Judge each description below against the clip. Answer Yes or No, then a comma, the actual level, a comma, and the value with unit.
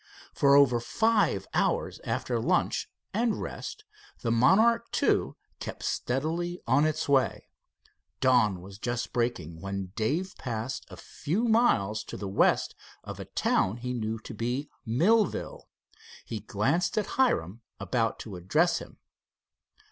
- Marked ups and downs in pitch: Yes, wide, 8.0 semitones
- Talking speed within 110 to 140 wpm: Yes, slow, 135 wpm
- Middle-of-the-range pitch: No, low, 125 Hz